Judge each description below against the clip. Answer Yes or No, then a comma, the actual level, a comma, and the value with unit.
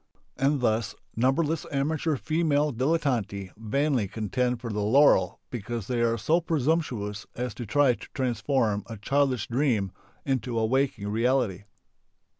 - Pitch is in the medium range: No, low, 125 Hz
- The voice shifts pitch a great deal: No, average, 4.5 semitones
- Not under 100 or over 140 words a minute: Yes, slow, 135 wpm